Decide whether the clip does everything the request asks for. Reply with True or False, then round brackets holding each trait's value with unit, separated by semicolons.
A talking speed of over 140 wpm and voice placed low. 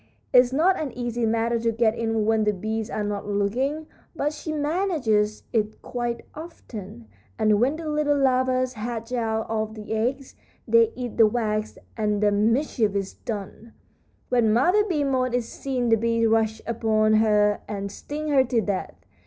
False (170 wpm; 230 Hz)